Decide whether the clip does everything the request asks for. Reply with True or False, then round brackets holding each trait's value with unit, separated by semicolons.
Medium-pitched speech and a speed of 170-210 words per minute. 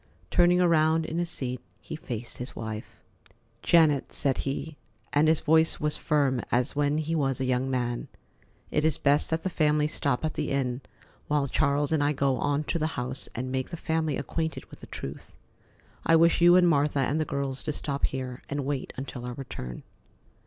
True (145 Hz; 195 wpm)